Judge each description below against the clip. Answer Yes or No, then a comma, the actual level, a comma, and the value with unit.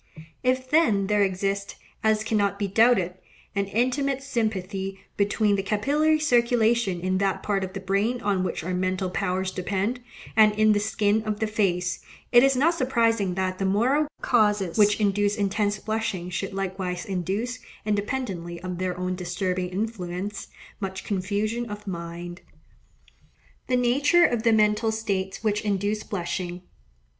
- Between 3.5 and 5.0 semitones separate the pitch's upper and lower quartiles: No, average, 3.0 semitones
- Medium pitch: No, high, 205 Hz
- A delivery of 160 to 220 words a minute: No, average, 150 wpm